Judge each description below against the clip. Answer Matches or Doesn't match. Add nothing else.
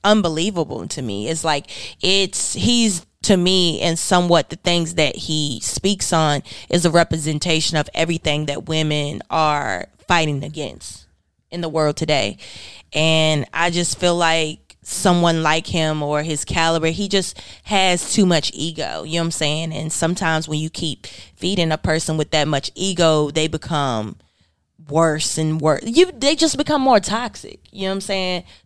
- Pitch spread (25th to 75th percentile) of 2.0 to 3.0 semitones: Matches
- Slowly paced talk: Doesn't match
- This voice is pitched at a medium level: Matches